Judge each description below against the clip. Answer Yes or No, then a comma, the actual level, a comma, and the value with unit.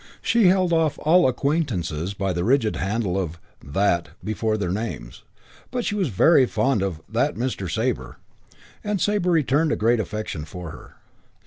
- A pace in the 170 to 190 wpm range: No, average, 160 wpm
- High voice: No, low, 110 Hz